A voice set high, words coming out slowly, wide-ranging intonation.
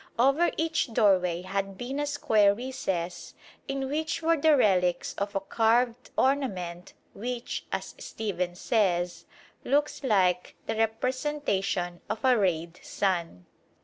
Yes: high, 215 Hz; slow, 125 wpm; wide, 6.5 semitones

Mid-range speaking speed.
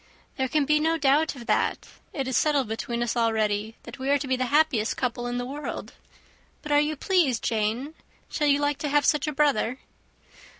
No: fast, 210 wpm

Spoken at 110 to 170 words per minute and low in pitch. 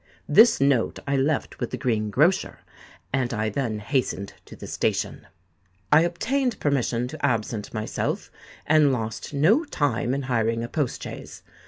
Yes: average, 155 wpm; low, 130 Hz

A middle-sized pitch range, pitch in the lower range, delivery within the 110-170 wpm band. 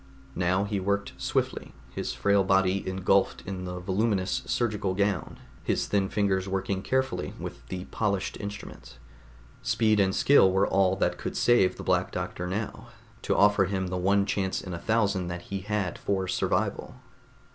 No: narrow, 1.5 semitones; very low, 95 Hz; average, 165 wpm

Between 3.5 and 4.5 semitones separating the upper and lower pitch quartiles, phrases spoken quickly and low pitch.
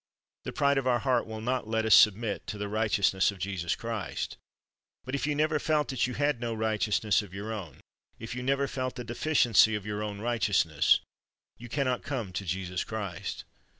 Yes: average, 4.1 semitones; fast, 210 wpm; low, 110 Hz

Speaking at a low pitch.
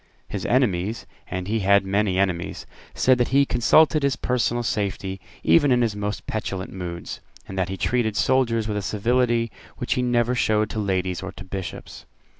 Yes: low, 105 Hz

